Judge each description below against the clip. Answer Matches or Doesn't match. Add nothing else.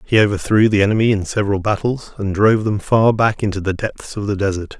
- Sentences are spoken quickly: Matches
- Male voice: Matches